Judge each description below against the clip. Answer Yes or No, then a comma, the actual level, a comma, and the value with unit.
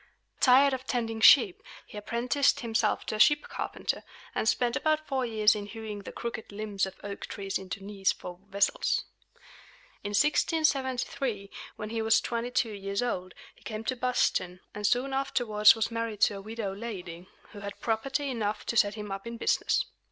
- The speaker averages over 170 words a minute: Yes, average, 180 wpm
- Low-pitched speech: No, high, 220 Hz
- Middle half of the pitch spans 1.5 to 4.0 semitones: Yes, average, 3.5 semitones